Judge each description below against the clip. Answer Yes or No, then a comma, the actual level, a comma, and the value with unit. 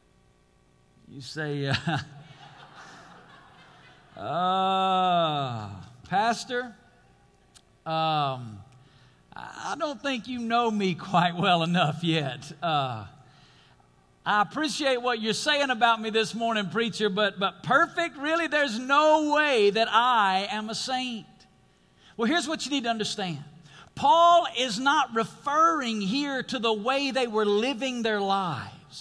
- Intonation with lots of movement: Yes, wide, 9.0 semitones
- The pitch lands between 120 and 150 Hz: No, high, 210 Hz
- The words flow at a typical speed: No, slow, 120 wpm